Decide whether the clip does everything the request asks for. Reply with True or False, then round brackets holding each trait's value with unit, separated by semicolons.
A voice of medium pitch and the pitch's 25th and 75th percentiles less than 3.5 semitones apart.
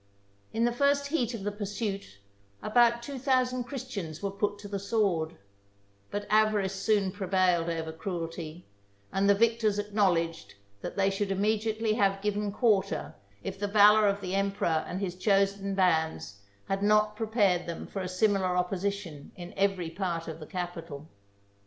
False (200 Hz; 2.9 semitones)